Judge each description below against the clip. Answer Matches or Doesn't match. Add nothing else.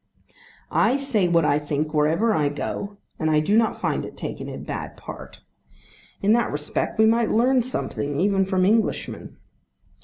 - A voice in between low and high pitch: Doesn't match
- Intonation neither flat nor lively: Doesn't match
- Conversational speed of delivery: Matches